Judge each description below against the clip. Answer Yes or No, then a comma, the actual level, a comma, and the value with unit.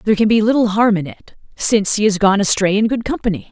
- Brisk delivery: Yes, fast, 255 wpm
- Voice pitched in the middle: No, high, 210 Hz